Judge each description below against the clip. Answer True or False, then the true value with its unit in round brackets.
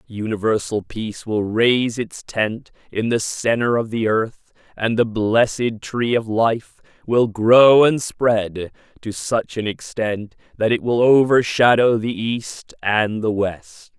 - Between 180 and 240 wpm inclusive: False (150 wpm)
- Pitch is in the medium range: False (110 Hz)